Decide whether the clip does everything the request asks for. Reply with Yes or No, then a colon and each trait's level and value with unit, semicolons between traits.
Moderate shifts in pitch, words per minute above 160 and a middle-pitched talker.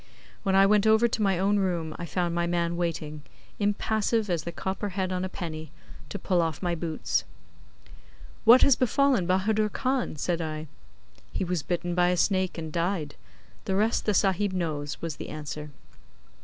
Yes: average, 3.5 semitones; average, 180 wpm; medium, 180 Hz